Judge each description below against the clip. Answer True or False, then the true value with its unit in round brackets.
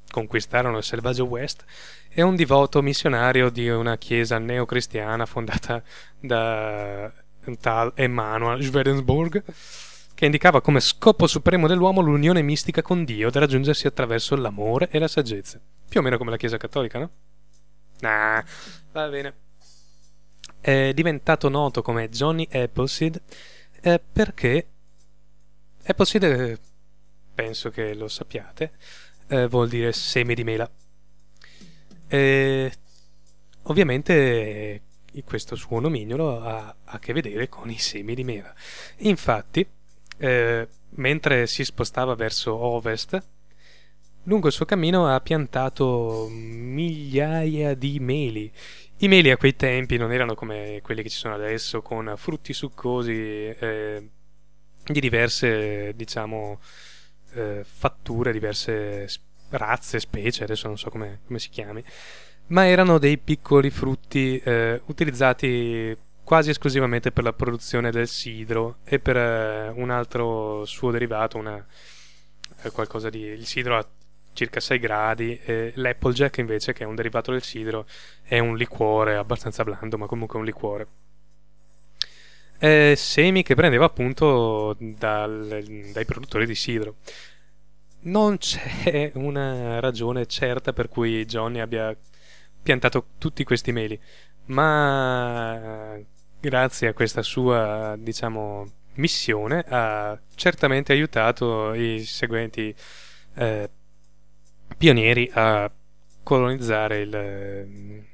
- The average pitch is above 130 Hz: False (120 Hz)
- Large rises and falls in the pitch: False (4.2 semitones)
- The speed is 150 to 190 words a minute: False (120 wpm)